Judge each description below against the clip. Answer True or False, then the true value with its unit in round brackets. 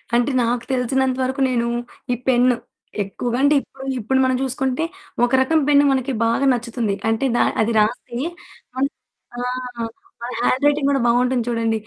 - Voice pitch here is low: False (250 Hz)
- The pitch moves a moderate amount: False (2.0 semitones)